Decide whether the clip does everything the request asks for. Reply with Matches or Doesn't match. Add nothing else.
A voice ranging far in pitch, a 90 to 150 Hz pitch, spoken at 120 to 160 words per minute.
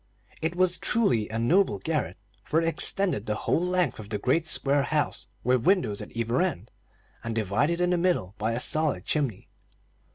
Doesn't match